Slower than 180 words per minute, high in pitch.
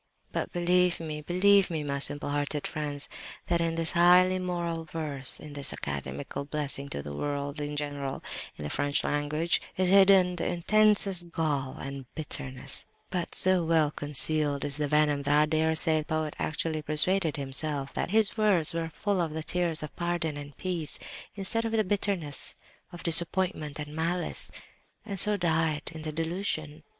No: average, 170 wpm; medium, 160 Hz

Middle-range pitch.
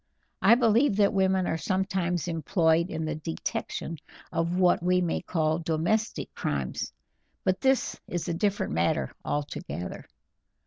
Yes: medium, 175 Hz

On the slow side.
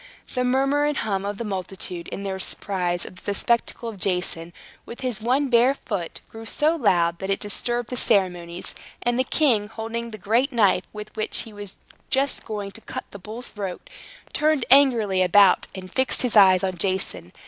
No: average, 190 wpm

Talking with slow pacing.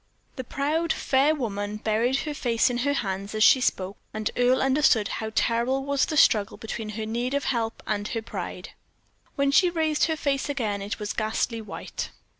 No: average, 190 wpm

